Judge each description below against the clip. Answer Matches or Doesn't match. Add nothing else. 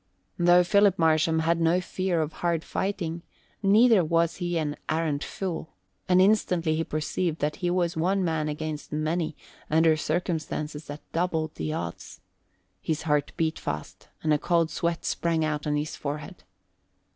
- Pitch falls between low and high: Matches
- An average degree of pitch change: Doesn't match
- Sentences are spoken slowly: Doesn't match